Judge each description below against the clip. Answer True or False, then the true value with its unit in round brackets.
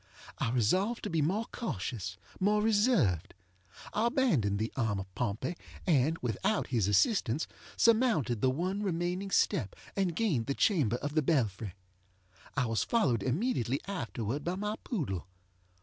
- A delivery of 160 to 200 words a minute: False (145 wpm)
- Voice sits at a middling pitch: True (150 Hz)